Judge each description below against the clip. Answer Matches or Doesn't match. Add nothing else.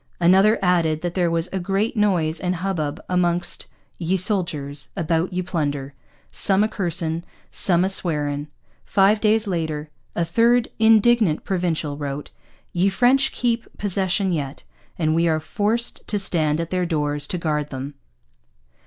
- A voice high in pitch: Doesn't match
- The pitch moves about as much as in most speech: Matches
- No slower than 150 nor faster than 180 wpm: Matches